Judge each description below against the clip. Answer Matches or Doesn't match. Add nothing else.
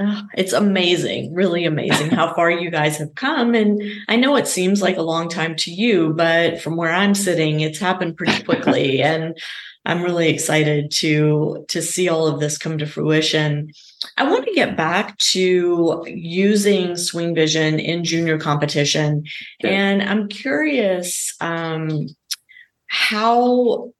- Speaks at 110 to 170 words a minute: Matches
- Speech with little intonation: Doesn't match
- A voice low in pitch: Doesn't match